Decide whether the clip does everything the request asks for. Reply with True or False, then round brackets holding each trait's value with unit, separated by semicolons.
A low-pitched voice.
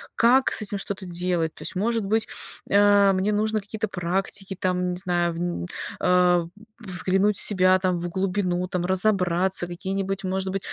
False (190 Hz)